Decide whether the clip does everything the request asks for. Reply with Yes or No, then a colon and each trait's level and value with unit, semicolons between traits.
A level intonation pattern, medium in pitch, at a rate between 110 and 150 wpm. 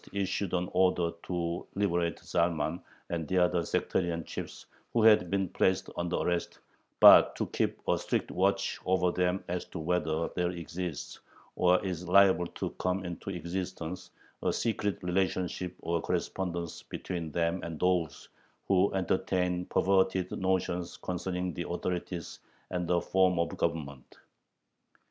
No: narrow, 1.5 semitones; very low, 90 Hz; average, 140 wpm